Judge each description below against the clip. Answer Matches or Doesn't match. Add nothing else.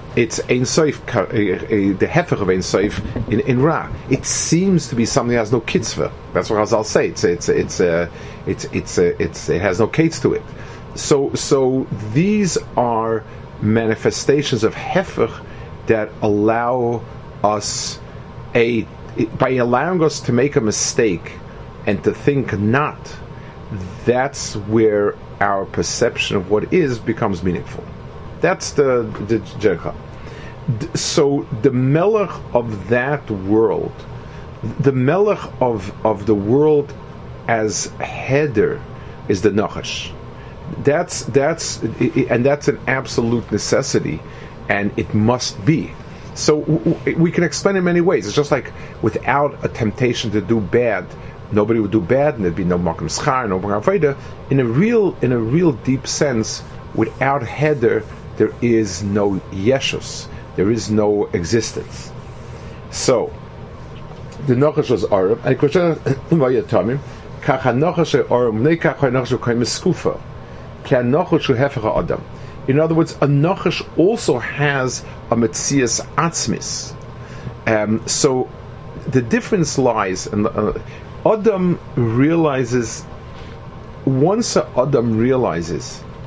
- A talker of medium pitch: Doesn't match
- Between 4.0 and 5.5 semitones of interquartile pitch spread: Matches